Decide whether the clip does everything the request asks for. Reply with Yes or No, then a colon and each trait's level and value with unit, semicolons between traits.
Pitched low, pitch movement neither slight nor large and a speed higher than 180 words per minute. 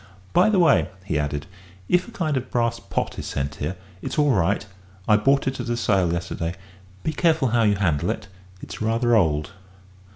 No: low, 110 Hz; wide, 8.2 semitones; average, 195 wpm